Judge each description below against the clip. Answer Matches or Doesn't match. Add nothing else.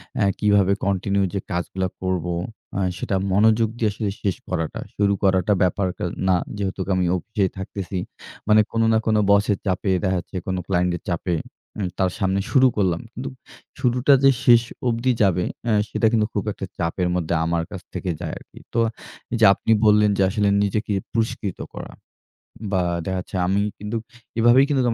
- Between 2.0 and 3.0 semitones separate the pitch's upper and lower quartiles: Matches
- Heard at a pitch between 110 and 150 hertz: Doesn't match